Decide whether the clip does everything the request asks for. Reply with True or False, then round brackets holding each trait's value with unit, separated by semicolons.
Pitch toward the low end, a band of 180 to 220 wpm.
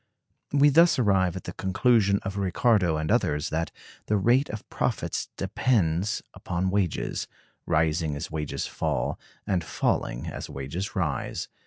False (95 Hz; 140 wpm)